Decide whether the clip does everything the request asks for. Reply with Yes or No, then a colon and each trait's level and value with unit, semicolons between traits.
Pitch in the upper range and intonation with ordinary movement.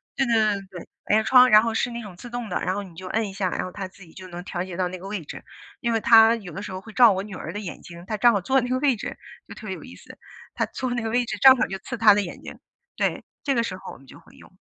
Yes: high, 210 Hz; average, 4.1 semitones